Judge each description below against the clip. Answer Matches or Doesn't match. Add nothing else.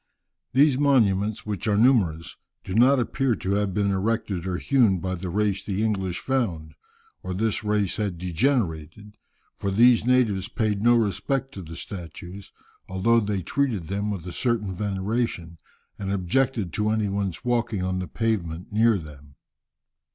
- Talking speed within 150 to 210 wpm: Matches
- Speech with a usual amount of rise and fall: Matches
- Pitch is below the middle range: Matches